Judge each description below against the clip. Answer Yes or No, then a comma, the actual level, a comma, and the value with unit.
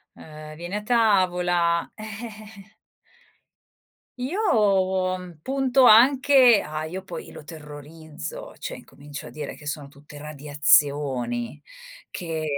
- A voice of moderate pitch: Yes, medium, 175 Hz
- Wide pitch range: Yes, wide, 6.4 semitones